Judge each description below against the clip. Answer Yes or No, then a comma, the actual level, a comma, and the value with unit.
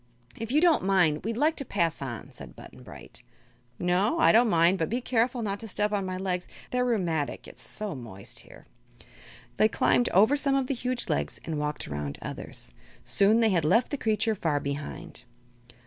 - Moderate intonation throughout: No, wide, 6.6 semitones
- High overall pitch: Yes, high, 200 Hz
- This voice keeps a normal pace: Yes, average, 195 wpm